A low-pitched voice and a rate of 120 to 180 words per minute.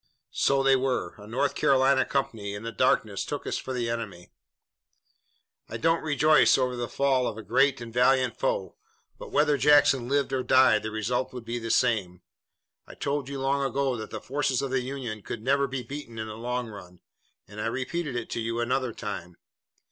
No: low, 125 Hz; average, 200 wpm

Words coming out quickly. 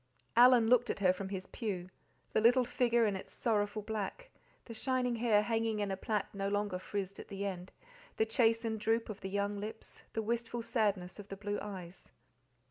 No: average, 195 wpm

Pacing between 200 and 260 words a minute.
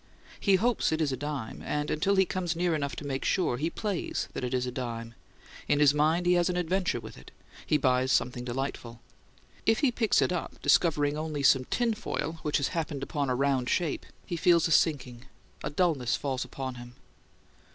Yes: fast, 205 wpm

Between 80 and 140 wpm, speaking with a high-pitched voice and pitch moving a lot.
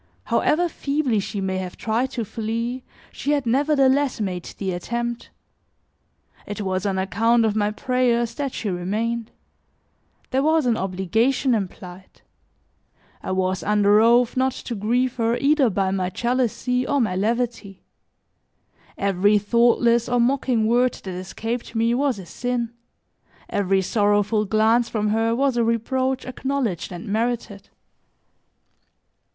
No: slow, 135 wpm; high, 230 Hz; average, 3.6 semitones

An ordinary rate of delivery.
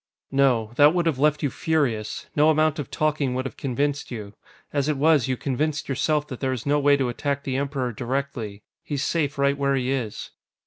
No: fast, 210 wpm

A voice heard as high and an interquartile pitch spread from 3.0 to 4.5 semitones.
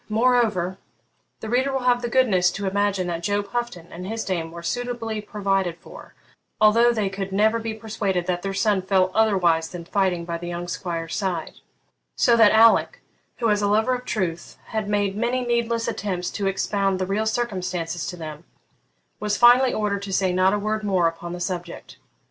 Yes: high, 200 Hz; average, 3.7 semitones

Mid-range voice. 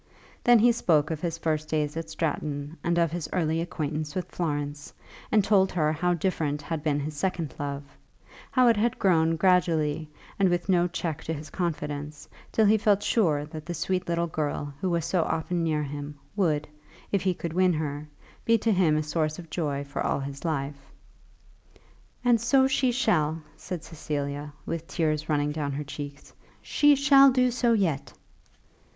Yes: medium, 160 Hz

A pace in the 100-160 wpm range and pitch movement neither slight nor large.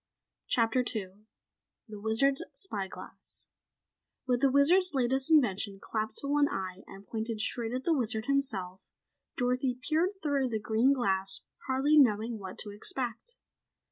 Yes: average, 140 wpm; average, 4.5 semitones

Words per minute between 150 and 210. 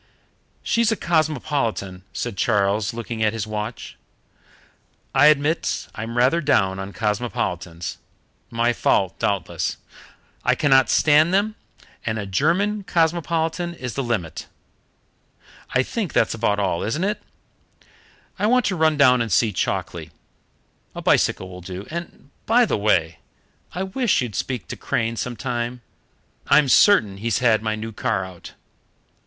No: average, 140 wpm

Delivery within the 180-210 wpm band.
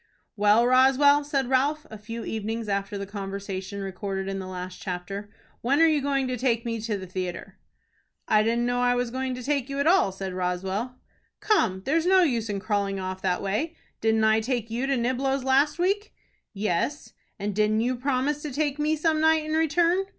Yes: average, 200 wpm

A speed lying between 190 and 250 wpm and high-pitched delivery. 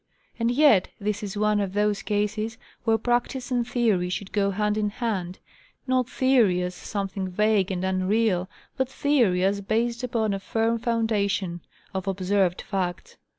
No: average, 150 wpm; high, 210 Hz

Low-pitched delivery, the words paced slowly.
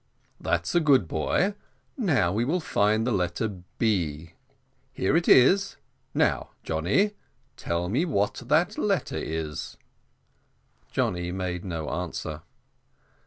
Yes: low, 100 Hz; slow, 120 wpm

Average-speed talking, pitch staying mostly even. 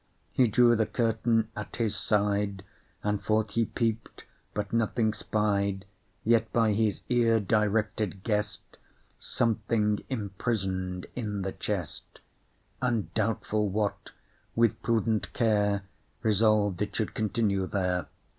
No: slow, 115 wpm; narrow, 2.0 semitones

